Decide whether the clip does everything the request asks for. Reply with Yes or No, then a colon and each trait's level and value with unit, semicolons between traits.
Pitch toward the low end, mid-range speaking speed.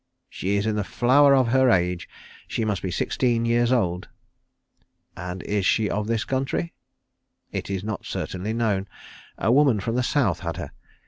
Yes: low, 110 Hz; average, 175 wpm